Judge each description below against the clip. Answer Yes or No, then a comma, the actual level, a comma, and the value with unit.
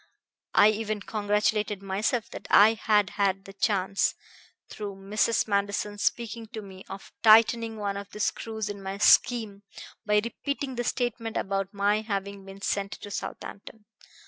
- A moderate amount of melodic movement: No, narrow, 1.8 semitones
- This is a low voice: No, high, 210 Hz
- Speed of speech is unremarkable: Yes, average, 150 wpm